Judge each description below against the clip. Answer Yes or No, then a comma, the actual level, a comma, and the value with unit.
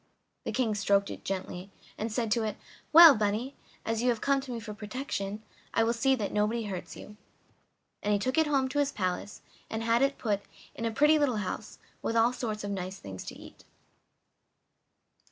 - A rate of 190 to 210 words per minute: Yes, average, 200 wpm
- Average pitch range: Yes, average, 3.8 semitones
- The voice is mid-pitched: No, high, 225 Hz